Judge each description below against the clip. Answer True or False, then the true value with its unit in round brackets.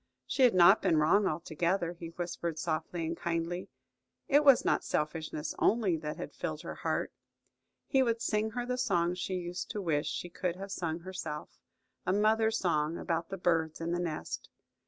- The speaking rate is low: False (175 wpm)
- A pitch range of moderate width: True (3.3 semitones)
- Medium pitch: True (175 Hz)